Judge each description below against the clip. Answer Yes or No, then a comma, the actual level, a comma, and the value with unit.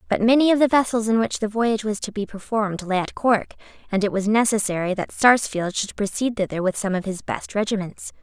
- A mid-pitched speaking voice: No, high, 215 Hz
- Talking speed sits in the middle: No, fast, 225 wpm